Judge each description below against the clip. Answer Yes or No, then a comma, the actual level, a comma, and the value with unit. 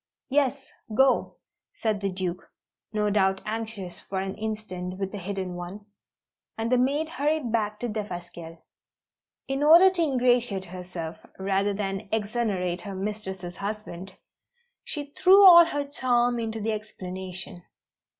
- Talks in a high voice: Yes, high, 210 Hz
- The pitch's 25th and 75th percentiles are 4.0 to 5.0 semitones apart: Yes, average, 4.5 semitones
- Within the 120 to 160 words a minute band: Yes, slow, 135 wpm